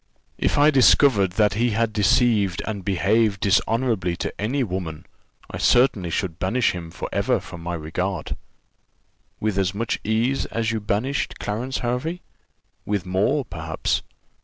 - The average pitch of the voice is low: Yes, low, 105 Hz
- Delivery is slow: No, average, 145 wpm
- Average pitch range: Yes, average, 4.6 semitones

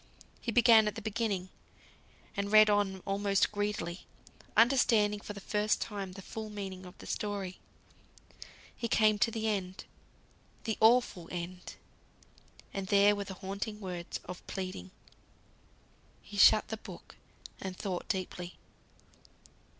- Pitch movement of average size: No, narrow, 2.3 semitones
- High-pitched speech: Yes, high, 200 Hz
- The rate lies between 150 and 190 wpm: No, slow, 135 wpm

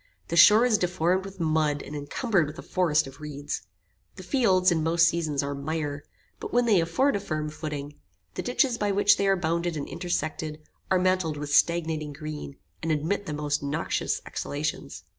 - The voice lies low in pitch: No, medium, 160 Hz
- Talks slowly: No, average, 185 wpm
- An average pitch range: Yes, average, 3.7 semitones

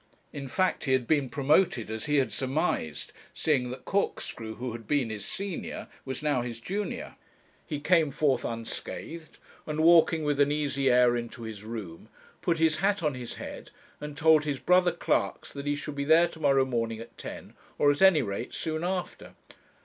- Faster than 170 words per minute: Yes, average, 190 wpm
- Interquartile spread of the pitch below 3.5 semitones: No, average, 4.6 semitones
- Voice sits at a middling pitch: Yes, medium, 145 Hz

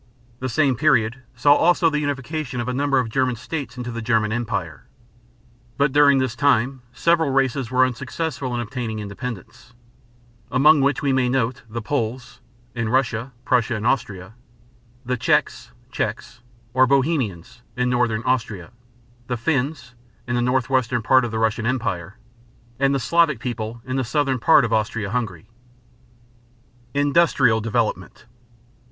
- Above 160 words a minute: No, average, 145 wpm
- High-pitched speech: No, low, 125 Hz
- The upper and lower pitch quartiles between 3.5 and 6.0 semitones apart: No, average, 3.1 semitones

